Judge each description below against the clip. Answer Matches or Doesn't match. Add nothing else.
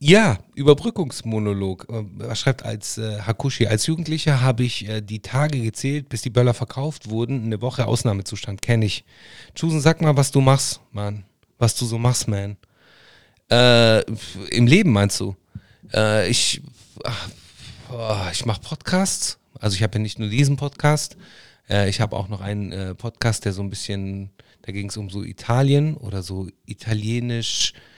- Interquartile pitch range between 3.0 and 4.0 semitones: Doesn't match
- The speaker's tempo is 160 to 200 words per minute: Matches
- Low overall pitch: Matches